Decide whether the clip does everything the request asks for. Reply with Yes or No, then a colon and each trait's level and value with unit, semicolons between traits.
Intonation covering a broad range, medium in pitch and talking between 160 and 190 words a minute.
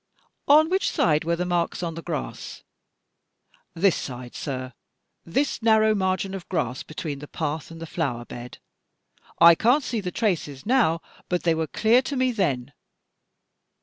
Yes: wide, 6.5 semitones; medium, 170 Hz; average, 165 wpm